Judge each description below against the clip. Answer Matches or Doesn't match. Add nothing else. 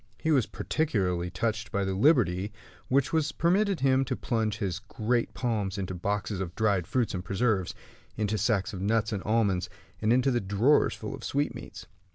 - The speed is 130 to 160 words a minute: Doesn't match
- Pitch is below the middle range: Matches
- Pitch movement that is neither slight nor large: Matches